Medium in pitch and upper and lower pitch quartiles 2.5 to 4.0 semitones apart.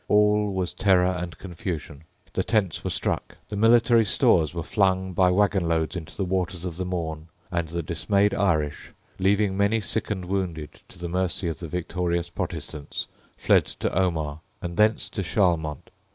No: very low, 90 Hz; average, 2.9 semitones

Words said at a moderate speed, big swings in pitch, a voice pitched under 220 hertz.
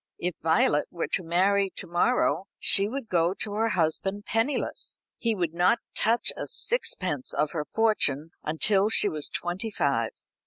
No: average, 160 wpm; average, 4.9 semitones; medium, 185 Hz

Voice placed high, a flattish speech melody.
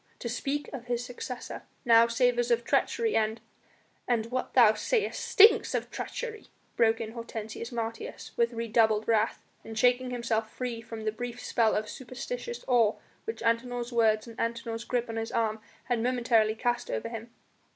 Yes: high, 235 Hz; narrow, 1.6 semitones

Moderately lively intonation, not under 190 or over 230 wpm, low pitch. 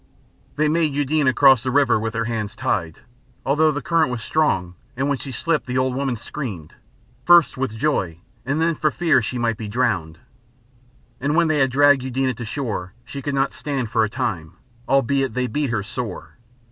Yes: average, 4.2 semitones; average, 195 wpm; low, 130 Hz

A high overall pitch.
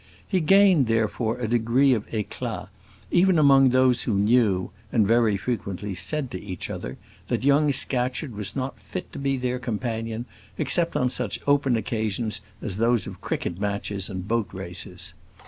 No: low, 120 Hz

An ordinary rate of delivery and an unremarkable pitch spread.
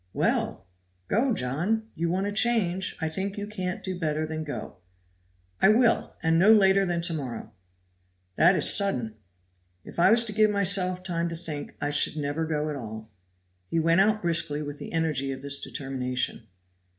Yes: average, 180 wpm; average, 5.0 semitones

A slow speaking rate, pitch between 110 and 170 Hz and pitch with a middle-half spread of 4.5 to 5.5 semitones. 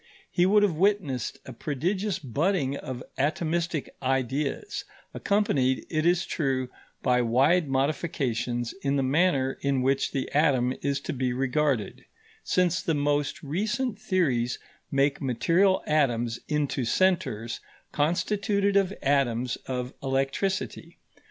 Yes: slow, 120 wpm; medium, 140 Hz; average, 5.1 semitones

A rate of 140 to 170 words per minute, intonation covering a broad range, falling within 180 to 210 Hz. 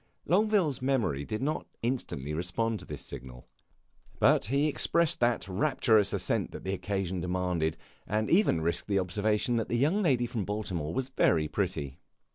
No: average, 160 wpm; wide, 6.8 semitones; low, 105 Hz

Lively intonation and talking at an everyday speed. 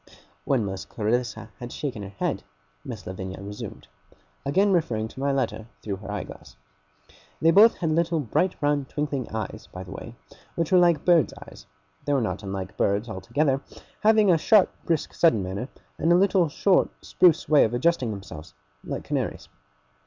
Yes: wide, 8.3 semitones; average, 175 wpm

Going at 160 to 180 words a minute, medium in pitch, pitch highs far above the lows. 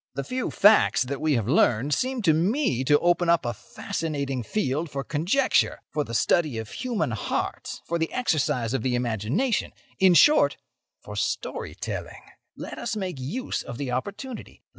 Yes: average, 165 wpm; medium, 150 Hz; wide, 7.8 semitones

